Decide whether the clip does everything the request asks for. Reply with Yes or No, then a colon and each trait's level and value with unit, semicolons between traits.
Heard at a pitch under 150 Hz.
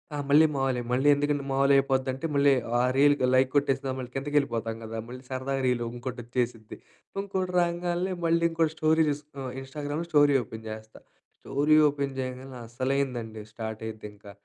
Yes: low, 135 Hz